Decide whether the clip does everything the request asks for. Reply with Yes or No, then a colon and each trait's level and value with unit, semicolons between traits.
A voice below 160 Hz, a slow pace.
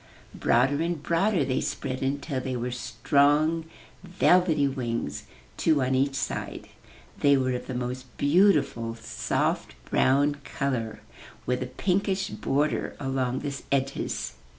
Yes: low, 135 Hz; slow, 130 wpm